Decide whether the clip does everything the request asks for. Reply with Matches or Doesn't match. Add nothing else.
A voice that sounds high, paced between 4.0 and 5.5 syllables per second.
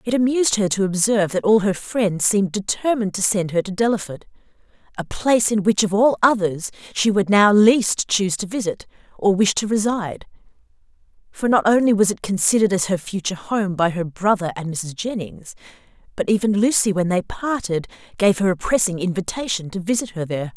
Doesn't match